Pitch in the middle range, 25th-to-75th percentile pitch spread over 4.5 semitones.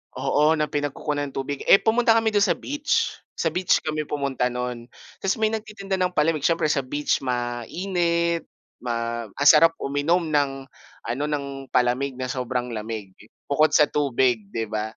Yes: medium, 145 Hz; average, 5.3 semitones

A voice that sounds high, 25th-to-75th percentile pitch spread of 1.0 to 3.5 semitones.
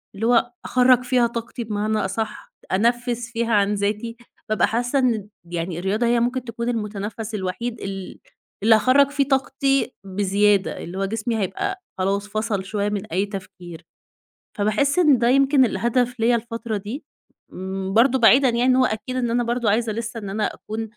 Yes: high, 225 Hz; average, 3.2 semitones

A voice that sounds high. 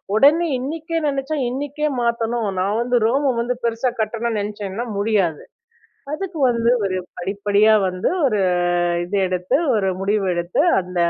Yes: high, 220 Hz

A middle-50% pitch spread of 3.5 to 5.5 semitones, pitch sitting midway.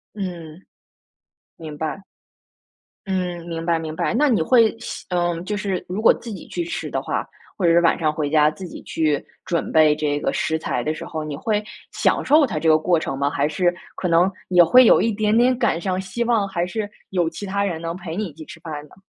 Yes: average, 4.2 semitones; medium, 175 Hz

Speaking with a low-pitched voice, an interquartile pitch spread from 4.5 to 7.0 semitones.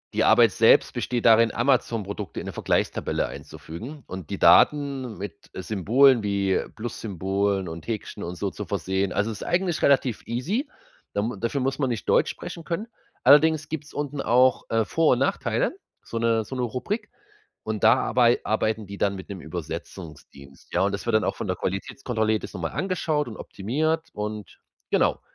Yes: low, 115 Hz; wide, 5.5 semitones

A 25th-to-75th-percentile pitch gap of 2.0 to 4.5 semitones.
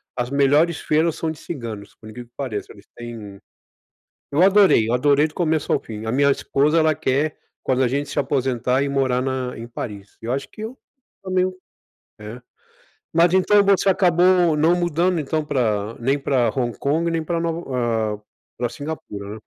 No: wide, 5.6 semitones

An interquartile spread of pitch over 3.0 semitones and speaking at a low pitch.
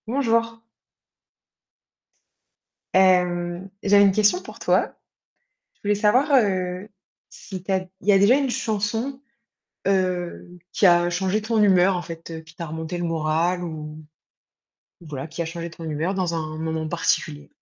No: average, 3.8 semitones; medium, 180 Hz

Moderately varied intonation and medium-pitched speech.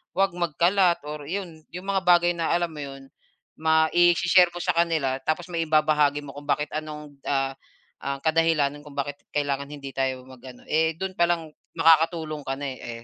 Yes: average, 3.2 semitones; medium, 155 Hz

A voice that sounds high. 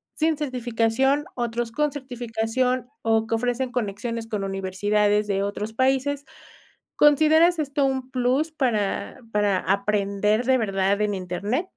Yes: high, 230 Hz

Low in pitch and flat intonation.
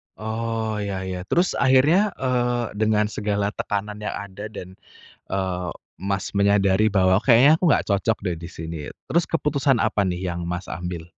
No: low, 105 Hz; average, 3.6 semitones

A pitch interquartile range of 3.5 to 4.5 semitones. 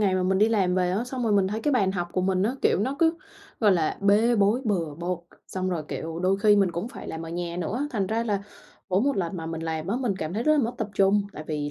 Yes: average, 4.0 semitones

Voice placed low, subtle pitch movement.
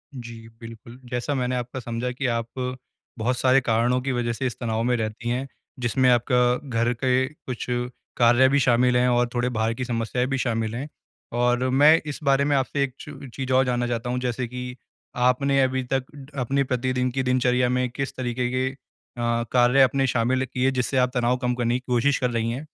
Yes: low, 125 Hz; narrow, 1.5 semitones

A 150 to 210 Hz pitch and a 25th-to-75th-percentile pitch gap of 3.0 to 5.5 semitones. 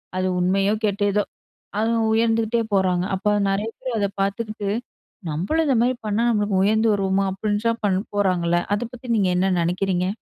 No: high, 205 Hz; narrow, 2.6 semitones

